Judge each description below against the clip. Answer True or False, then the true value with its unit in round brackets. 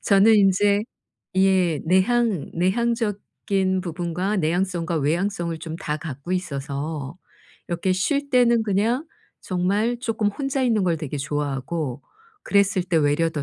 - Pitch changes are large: False (4.3 semitones)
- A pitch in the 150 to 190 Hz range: True (185 Hz)